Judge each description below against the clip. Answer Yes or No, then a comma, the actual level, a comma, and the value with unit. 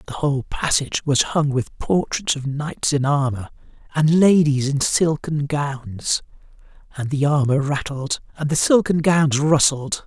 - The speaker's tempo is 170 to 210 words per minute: No, average, 150 wpm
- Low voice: No, medium, 145 Hz